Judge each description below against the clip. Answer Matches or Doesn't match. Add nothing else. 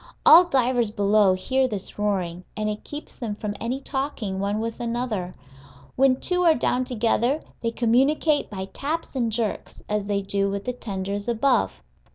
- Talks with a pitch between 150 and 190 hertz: Doesn't match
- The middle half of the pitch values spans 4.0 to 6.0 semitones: Matches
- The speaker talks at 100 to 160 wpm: Doesn't match